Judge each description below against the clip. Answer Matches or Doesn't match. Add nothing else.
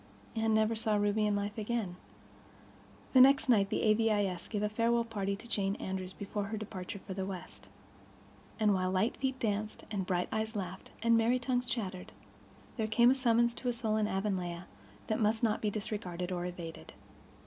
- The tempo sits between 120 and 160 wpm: Doesn't match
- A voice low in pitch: Doesn't match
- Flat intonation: Doesn't match